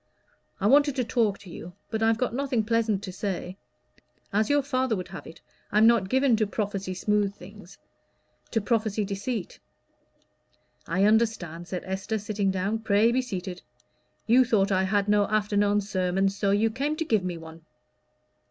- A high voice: Yes, high, 205 Hz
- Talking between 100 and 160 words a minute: No, average, 170 wpm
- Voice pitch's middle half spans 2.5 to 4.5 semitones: Yes, average, 2.9 semitones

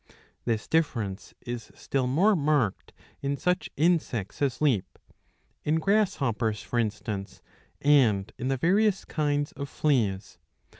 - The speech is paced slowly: Yes, slow, 120 wpm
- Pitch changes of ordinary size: No, wide, 5.9 semitones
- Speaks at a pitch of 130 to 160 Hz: Yes, low, 135 Hz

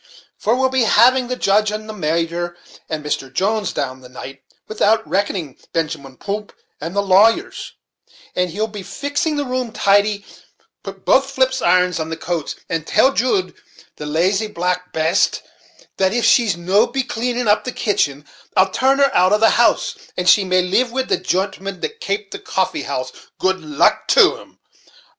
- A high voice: Yes, high, 200 Hz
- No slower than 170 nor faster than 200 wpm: Yes, average, 180 wpm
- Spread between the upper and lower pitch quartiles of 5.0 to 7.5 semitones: Yes, wide, 5.4 semitones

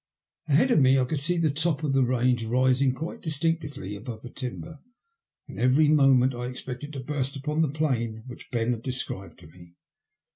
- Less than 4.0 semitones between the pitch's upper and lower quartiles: Yes, average, 3.4 semitones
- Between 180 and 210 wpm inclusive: Yes, average, 190 wpm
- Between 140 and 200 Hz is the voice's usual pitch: No, low, 130 Hz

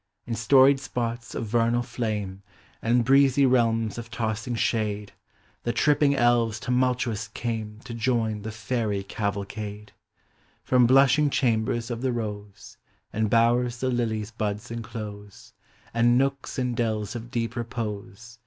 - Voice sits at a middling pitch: No, low, 115 Hz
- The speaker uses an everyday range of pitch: No, narrow, 2.1 semitones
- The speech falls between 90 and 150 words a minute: Yes, slow, 135 wpm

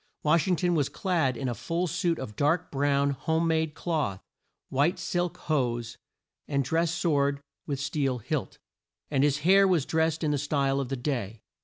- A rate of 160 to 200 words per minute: Yes, average, 180 wpm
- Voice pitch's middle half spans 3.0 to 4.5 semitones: Yes, average, 3.4 semitones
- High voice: No, medium, 150 Hz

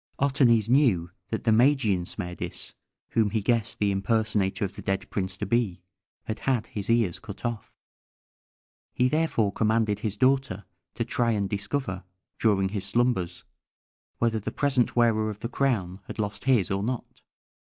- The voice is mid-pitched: No, low, 110 Hz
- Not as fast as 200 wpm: Yes, average, 160 wpm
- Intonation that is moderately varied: Yes, average, 3.5 semitones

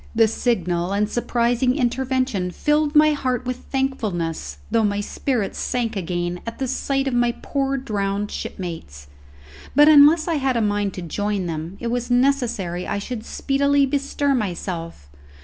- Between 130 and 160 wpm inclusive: Yes, average, 155 wpm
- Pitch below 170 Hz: No, high, 235 Hz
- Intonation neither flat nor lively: No, wide, 5.8 semitones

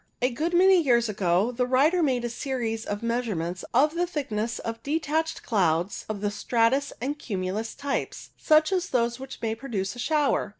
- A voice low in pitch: No, high, 245 Hz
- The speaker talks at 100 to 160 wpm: No, average, 180 wpm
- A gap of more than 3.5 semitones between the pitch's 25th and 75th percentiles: Yes, average, 5.1 semitones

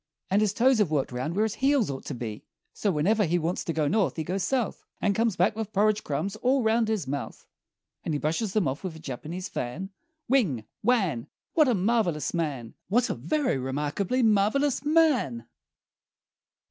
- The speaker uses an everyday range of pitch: No, wide, 6.9 semitones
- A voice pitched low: No, high, 195 Hz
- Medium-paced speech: Yes, average, 190 wpm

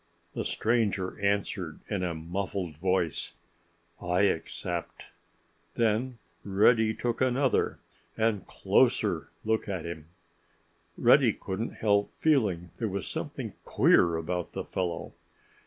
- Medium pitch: No, low, 100 Hz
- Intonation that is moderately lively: Yes, average, 4.1 semitones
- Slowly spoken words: Yes, slow, 105 wpm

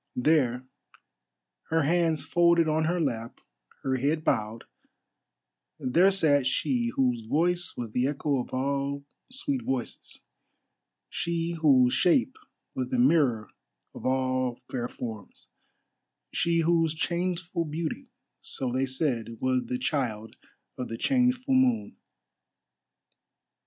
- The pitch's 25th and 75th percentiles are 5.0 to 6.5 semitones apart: Yes, average, 5.3 semitones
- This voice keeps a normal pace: No, slow, 115 wpm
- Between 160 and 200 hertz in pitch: No, medium, 145 Hz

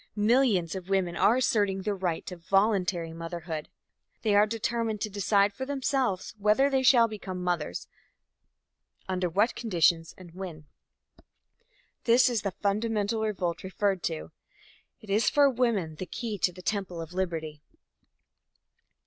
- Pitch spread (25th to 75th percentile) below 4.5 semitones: Yes, average, 4.0 semitones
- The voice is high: Yes, high, 195 Hz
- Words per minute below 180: Yes, average, 140 wpm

